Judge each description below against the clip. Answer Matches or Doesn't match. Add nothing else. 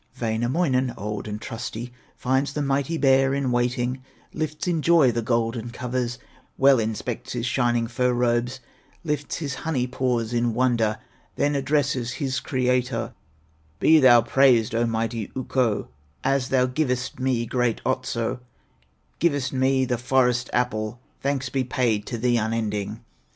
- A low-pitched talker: Matches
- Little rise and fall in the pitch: Matches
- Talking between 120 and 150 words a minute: Matches